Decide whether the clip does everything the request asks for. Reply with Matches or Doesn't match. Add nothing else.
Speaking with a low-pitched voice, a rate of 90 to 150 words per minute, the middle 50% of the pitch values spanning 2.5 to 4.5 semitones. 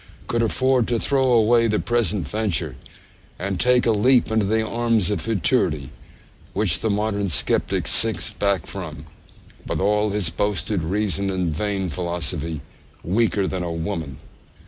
Matches